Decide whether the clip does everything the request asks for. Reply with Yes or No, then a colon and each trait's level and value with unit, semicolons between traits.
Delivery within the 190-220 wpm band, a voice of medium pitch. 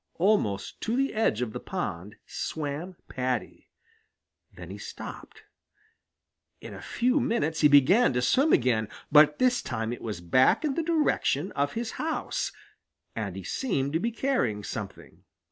No: average, 155 wpm; medium, 150 Hz